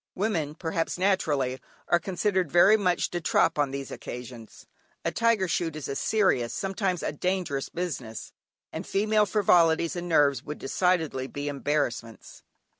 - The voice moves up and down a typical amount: Yes, average, 5.0 semitones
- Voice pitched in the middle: Yes, medium, 165 Hz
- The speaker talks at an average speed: Yes, average, 145 wpm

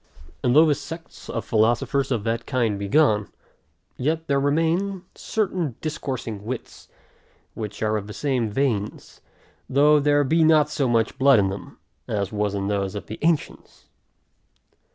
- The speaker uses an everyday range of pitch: No, wide, 6.0 semitones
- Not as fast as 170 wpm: Yes, average, 155 wpm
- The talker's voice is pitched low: Yes, low, 130 Hz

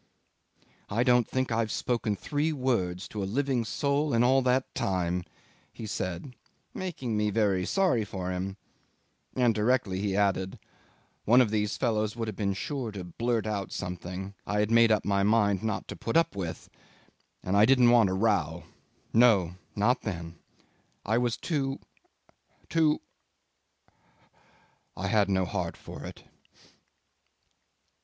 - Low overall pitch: Yes, low, 110 Hz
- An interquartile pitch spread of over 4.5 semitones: No, average, 4.2 semitones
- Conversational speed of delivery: Yes, average, 150 wpm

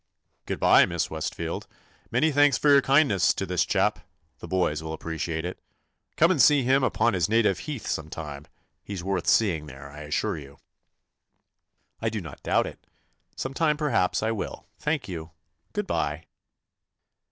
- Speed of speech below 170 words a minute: No, average, 175 wpm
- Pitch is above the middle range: No, very low, 95 Hz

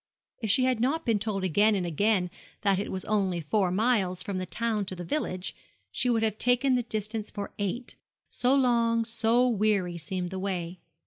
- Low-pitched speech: No, high, 210 Hz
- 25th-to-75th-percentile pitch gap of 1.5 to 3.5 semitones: No, average, 3.9 semitones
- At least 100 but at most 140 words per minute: No, average, 195 wpm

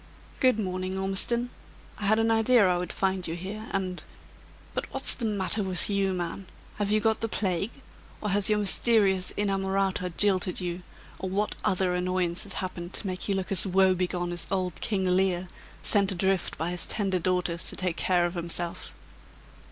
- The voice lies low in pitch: No, high, 190 Hz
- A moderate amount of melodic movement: No, narrow, 2.0 semitones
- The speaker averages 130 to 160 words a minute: No, average, 180 wpm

